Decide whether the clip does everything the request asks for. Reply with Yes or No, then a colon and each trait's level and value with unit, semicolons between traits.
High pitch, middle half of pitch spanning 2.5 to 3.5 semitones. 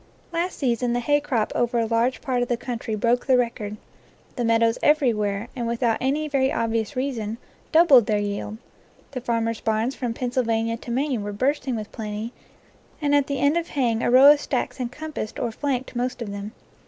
Yes: high, 240 Hz; average, 3.0 semitones